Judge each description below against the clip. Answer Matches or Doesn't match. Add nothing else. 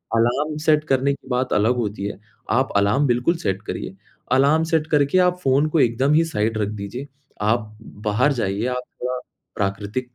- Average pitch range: Matches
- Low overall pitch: Matches